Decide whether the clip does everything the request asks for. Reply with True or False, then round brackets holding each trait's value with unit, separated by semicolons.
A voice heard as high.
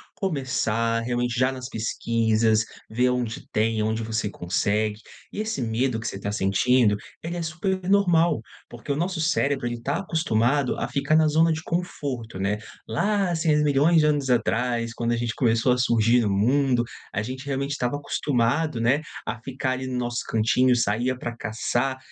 False (125 Hz)